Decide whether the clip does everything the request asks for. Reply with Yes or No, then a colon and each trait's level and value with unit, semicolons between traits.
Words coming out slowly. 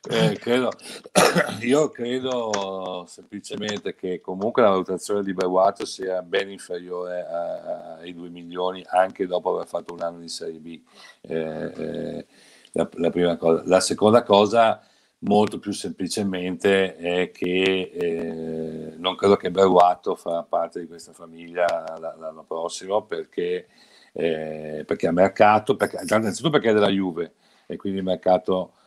No: average, 140 wpm